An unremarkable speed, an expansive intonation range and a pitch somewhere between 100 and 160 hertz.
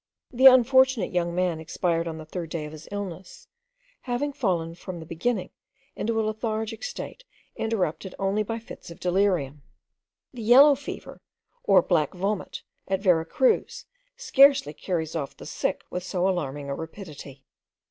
No: average, 155 wpm; wide, 5.7 semitones; medium, 185 Hz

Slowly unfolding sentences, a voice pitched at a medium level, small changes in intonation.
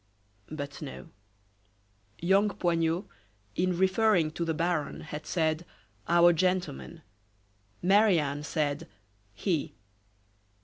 No: slow, 95 wpm; medium, 170 Hz; average, 3.1 semitones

